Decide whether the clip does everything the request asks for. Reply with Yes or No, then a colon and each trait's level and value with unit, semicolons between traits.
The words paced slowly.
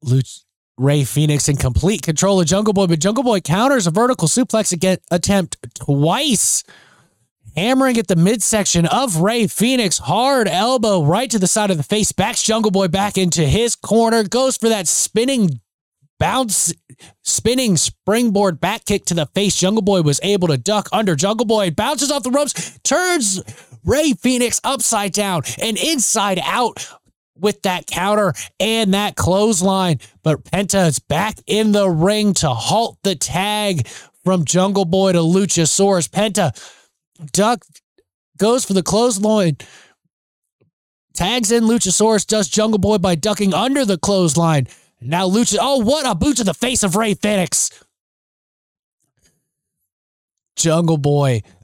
No: average, 145 wpm